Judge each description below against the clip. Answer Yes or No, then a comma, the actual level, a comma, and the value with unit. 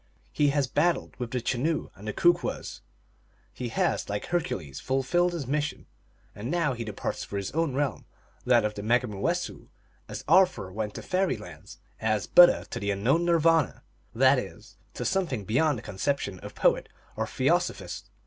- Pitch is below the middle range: Yes, low, 130 Hz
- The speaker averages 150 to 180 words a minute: Yes, average, 165 wpm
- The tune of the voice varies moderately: No, wide, 7.3 semitones